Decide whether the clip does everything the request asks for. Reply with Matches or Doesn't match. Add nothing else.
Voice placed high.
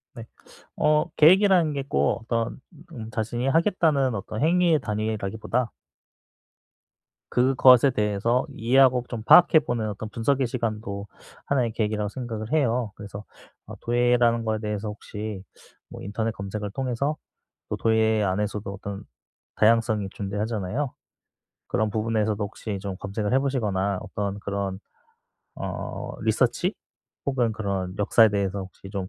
Doesn't match